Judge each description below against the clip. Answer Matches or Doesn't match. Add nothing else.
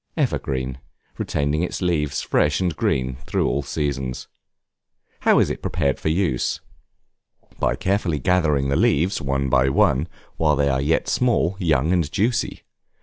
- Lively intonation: Doesn't match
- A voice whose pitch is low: Matches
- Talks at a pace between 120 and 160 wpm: Matches